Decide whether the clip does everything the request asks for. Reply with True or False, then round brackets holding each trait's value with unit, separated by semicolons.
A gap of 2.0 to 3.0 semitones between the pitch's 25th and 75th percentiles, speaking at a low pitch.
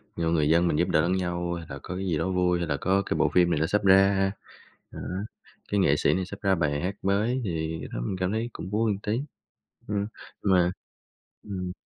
True (2.6 semitones; 90 Hz)